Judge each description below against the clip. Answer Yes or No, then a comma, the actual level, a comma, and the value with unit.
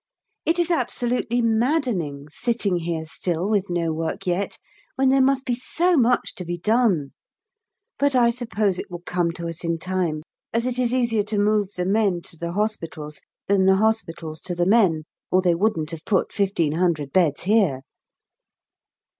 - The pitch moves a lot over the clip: Yes, wide, 5.7 semitones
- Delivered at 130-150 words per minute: No, average, 170 wpm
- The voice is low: No, high, 190 Hz